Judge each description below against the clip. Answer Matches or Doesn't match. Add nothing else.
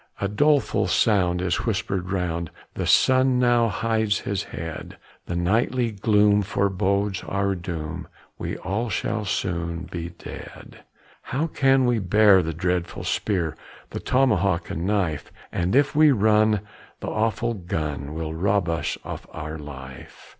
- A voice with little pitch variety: Doesn't match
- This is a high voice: Doesn't match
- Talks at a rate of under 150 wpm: Matches